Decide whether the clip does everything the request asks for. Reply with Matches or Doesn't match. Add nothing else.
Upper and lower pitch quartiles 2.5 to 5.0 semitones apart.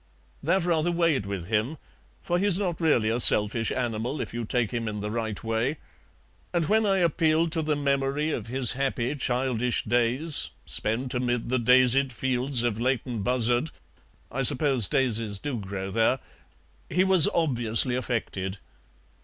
Matches